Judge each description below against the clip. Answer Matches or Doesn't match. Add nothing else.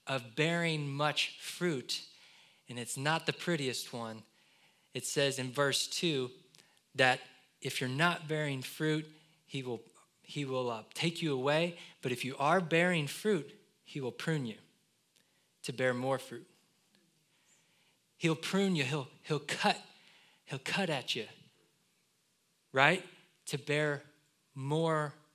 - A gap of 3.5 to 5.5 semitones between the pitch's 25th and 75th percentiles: Matches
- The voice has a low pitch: Doesn't match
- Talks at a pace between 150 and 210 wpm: Doesn't match